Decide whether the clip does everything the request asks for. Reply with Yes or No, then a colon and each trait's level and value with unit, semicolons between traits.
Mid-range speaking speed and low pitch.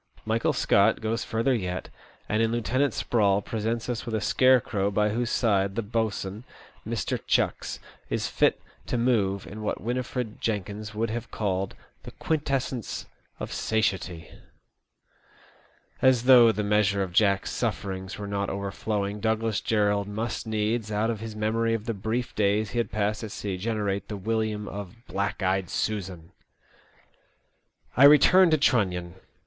Yes: average, 155 wpm; low, 110 Hz